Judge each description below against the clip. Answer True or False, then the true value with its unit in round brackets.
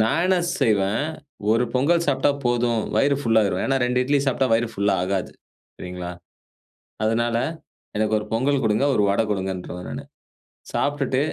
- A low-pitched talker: True (115 Hz)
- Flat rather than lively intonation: False (4.8 semitones)